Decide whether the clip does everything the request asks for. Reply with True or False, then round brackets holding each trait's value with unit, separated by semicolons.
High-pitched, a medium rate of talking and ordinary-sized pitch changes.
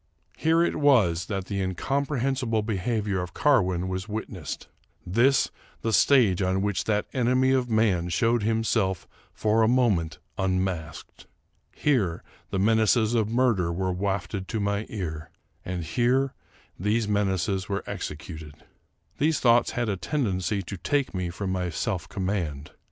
False (105 Hz; 145 wpm; 4.2 semitones)